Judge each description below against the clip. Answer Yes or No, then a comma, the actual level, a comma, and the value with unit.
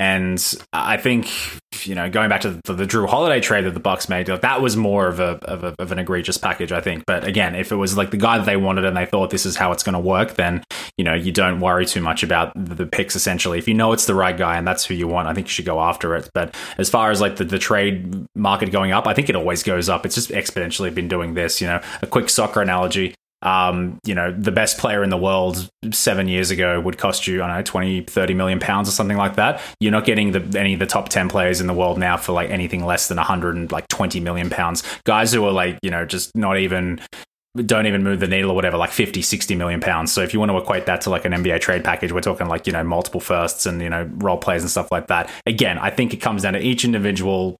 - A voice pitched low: Yes, very low, 95 Hz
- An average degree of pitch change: No, narrow, 2.0 semitones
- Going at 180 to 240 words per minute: No, fast, 280 wpm